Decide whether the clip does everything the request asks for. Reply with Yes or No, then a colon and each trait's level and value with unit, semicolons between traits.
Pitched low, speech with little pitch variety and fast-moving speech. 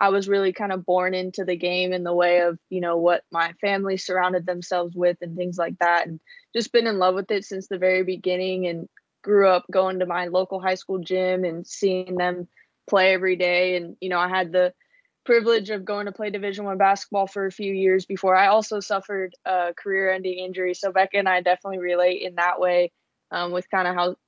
No: medium, 185 Hz; narrow, 1.6 semitones; fast, 225 wpm